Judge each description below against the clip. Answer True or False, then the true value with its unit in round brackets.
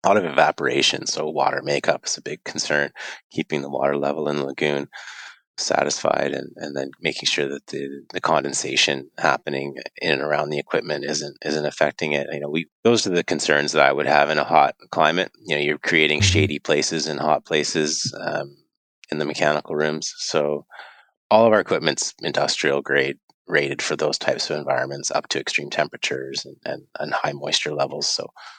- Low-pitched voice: True (75 Hz)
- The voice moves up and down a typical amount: False (1.8 semitones)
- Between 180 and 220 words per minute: True (190 wpm)